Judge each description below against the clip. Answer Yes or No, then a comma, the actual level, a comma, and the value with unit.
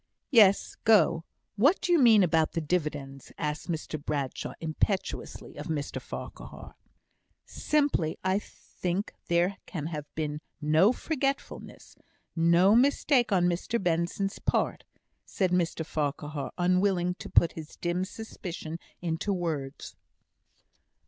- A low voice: No, medium, 175 Hz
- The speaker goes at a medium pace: No, slow, 120 wpm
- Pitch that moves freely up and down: No, average, 4.1 semitones